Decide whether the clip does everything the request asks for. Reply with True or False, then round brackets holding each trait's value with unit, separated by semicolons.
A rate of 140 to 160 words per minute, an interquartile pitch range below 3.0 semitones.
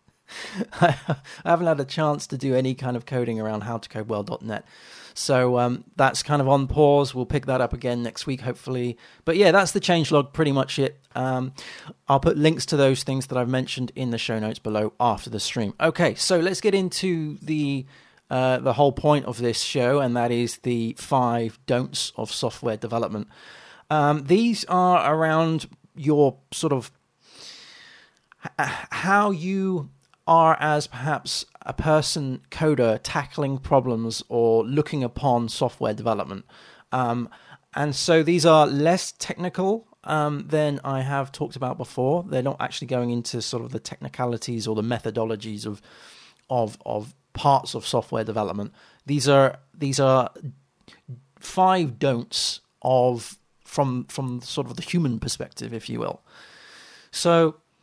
False (155 wpm; 4.1 semitones)